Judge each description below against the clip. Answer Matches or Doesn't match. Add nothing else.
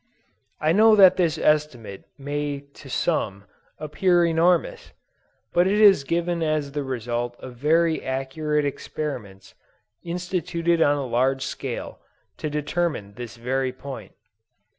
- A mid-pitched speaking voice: Matches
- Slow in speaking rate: Matches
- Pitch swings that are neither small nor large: Matches